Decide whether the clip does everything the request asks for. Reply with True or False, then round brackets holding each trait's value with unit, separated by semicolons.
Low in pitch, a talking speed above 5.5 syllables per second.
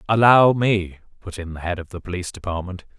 True (95 Hz; 6.0 syllables/s)